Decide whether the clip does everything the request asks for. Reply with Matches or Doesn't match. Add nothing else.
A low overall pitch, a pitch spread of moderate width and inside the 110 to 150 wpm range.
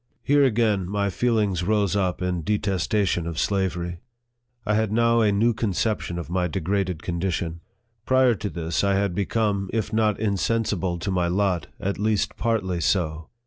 Doesn't match